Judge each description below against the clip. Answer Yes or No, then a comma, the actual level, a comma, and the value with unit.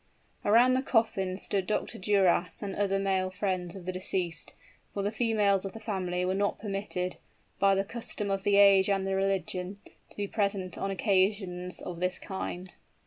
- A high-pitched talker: Yes, high, 195 Hz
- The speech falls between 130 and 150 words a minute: No, average, 180 wpm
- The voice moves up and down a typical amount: No, narrow, 1.7 semitones